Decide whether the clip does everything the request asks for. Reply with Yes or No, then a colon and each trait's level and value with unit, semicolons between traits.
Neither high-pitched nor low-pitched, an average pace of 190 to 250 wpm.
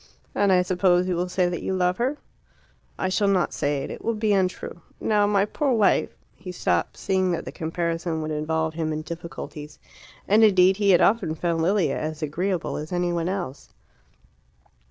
Yes: medium, 180 Hz; average, 195 wpm